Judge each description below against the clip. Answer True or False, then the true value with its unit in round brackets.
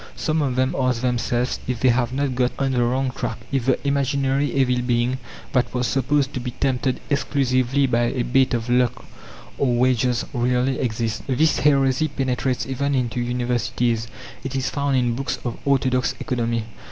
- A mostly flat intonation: True (1.8 semitones)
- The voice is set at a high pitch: False (130 Hz)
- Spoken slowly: False (175 wpm)